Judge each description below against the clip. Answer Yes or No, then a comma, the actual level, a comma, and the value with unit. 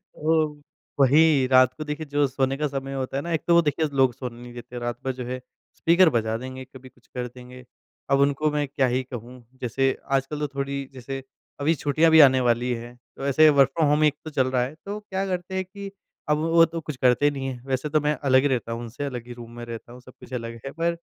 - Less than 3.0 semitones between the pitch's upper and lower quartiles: No, average, 3.3 semitones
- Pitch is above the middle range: No, low, 135 Hz